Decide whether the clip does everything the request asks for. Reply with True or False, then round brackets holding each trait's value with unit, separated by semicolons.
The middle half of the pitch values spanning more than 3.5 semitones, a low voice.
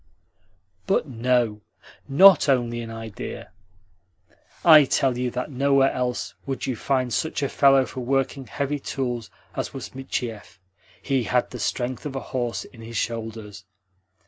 False (2.7 semitones; 125 Hz)